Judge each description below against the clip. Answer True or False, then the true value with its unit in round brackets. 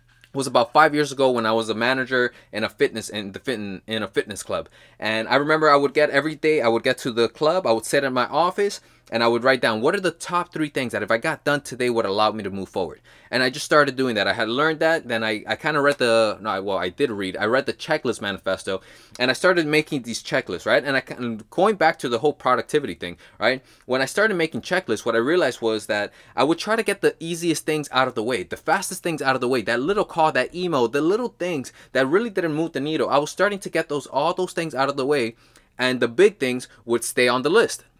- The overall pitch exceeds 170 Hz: False (135 Hz)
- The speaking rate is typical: False (275 wpm)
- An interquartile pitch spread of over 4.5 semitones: True (5.2 semitones)